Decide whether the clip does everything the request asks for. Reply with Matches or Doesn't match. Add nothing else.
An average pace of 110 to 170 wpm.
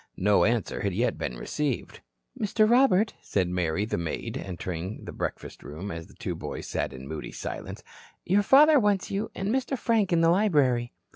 Doesn't match